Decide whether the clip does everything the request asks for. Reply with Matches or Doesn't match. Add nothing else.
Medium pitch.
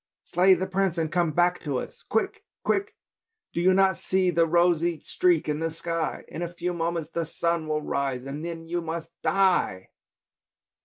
Matches